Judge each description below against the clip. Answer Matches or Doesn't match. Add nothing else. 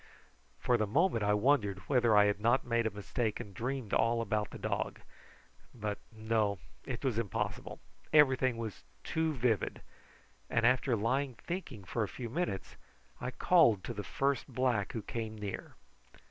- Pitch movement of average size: Matches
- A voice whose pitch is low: Matches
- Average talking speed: Matches